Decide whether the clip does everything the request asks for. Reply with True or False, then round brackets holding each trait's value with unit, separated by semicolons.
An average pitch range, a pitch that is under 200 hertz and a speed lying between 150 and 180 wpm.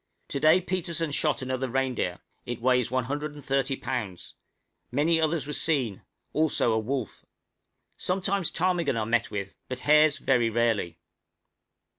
False (4.8 semitones; 135 Hz; 140 wpm)